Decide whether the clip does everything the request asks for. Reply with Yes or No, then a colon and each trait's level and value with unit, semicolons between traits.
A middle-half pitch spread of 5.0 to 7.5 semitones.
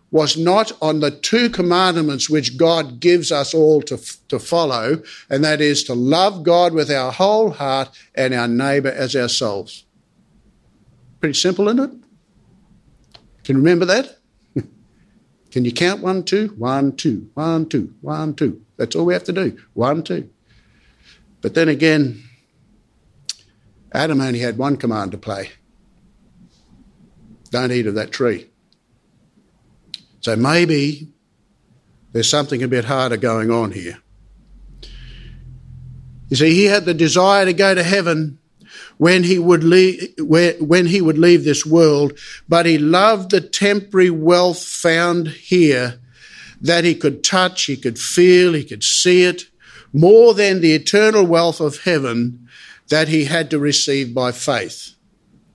Yes: wide, 5.5 semitones